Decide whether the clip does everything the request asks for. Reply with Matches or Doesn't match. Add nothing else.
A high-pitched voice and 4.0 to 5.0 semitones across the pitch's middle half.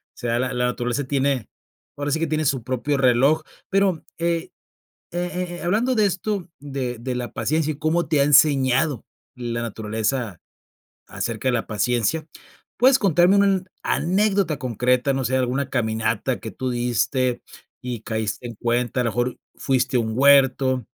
Doesn't match